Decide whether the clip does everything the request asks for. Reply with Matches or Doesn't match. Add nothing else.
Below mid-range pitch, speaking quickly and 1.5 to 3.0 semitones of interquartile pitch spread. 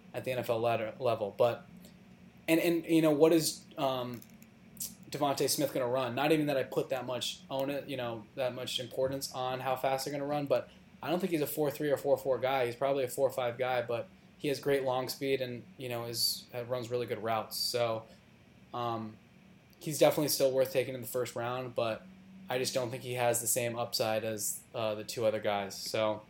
Matches